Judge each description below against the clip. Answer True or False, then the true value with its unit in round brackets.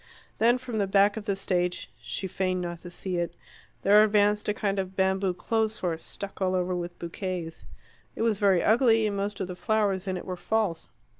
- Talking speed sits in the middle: False (210 wpm)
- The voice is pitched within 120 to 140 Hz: False (195 Hz)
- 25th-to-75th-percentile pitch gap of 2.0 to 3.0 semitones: True (2.6 semitones)